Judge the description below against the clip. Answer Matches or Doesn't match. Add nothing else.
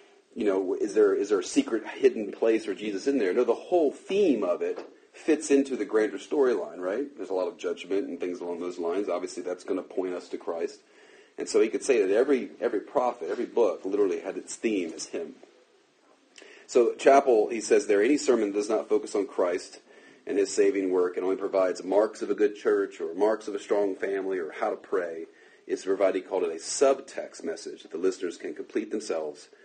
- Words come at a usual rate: Doesn't match